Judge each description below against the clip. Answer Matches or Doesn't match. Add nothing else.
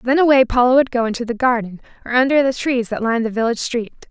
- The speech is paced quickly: Matches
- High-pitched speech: Matches